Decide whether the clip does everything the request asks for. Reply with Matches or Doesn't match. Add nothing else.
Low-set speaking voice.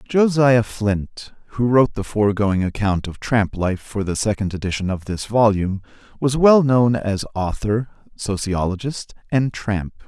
Matches